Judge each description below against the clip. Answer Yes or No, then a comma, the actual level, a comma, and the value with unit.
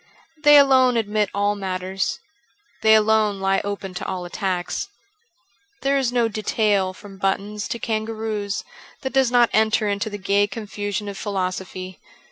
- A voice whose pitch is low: No, high, 205 Hz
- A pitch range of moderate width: No, narrow, 2.3 semitones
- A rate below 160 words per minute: Yes, average, 150 wpm